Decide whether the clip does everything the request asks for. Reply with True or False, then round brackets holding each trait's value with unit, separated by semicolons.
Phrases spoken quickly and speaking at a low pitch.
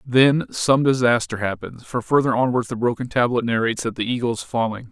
False (195 wpm; 120 Hz)